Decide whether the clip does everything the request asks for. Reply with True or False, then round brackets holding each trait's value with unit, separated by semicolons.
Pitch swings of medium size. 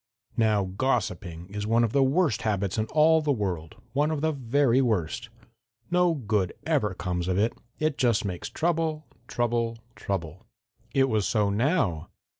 False (6.3 semitones)